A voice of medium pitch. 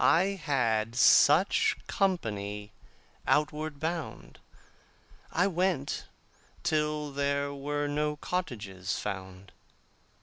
Yes: medium, 145 Hz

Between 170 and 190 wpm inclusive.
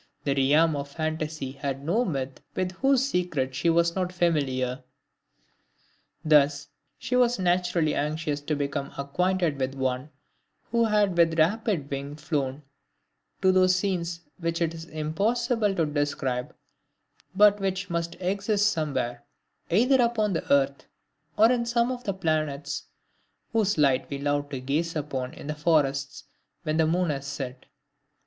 No: average, 145 wpm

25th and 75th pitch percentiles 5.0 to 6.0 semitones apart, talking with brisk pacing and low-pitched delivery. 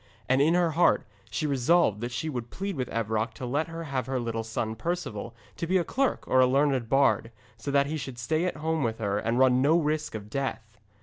Yes: wide, 5.4 semitones; fast, 235 wpm; low, 130 Hz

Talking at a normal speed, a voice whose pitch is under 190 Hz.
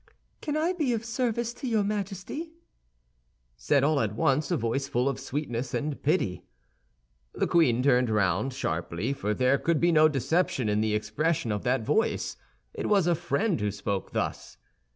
Yes: average, 175 wpm; medium, 140 Hz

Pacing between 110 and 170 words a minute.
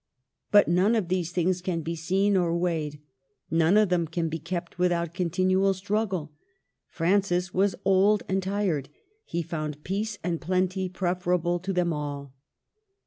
Yes: average, 150 wpm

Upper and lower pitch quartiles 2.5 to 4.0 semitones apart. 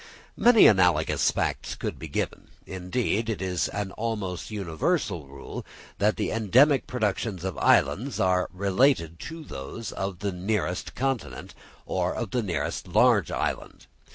No: average, 4.4 semitones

